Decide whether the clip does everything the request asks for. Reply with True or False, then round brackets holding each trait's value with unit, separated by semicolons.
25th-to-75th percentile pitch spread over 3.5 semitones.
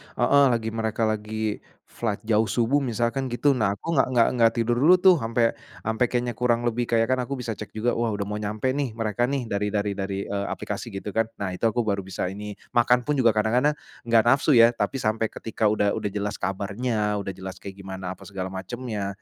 False (2.9 semitones)